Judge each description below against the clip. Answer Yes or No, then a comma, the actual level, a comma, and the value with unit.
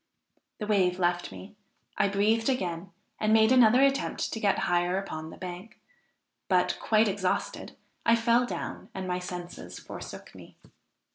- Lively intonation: No, average, 3.8 semitones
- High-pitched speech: Yes, high, 195 Hz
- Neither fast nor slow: Yes, average, 150 wpm